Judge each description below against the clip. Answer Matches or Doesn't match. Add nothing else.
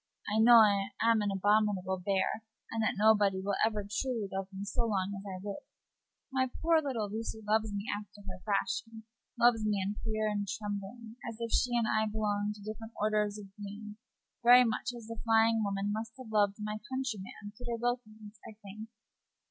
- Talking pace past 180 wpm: Matches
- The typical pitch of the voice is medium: Doesn't match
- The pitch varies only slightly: Matches